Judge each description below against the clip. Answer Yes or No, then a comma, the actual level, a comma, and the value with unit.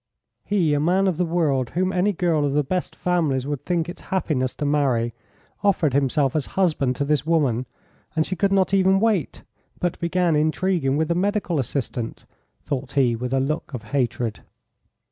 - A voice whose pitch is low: No, medium, 155 Hz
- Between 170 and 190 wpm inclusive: Yes, average, 185 wpm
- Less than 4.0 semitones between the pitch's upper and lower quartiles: No, average, 5.0 semitones